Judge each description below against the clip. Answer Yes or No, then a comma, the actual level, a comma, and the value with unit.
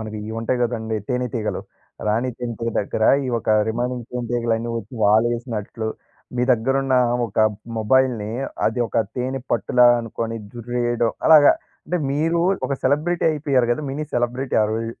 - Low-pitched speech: Yes, low, 120 Hz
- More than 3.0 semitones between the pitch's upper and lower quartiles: No, narrow, 2.5 semitones